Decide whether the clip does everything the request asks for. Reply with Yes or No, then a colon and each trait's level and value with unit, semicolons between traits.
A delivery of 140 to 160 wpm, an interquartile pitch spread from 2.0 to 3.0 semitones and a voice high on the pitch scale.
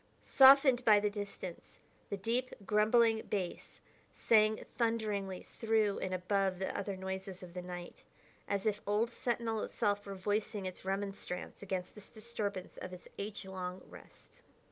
Yes: average, 145 wpm; average, 2.7 semitones; high, 205 Hz